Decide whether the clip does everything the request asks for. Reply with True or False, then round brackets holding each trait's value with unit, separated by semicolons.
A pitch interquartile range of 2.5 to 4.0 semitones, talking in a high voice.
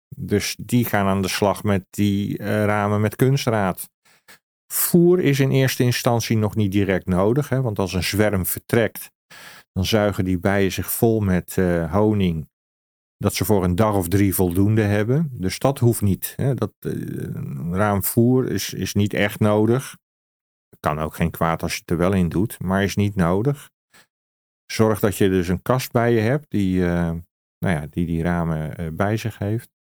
False (3.5 semitones; 100 Hz)